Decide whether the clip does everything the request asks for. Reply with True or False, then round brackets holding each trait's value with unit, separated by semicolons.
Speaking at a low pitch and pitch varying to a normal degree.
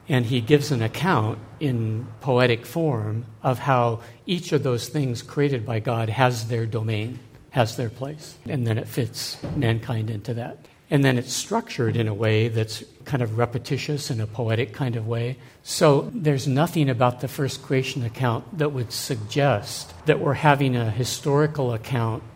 True (125 Hz; 3.5 semitones)